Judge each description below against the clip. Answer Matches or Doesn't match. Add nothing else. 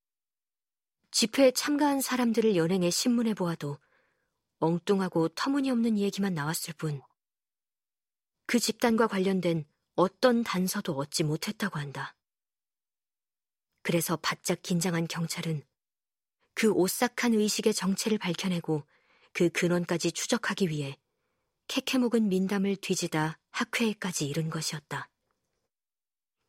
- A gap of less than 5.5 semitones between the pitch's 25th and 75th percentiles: Matches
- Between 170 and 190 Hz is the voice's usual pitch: Matches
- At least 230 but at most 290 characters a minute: Matches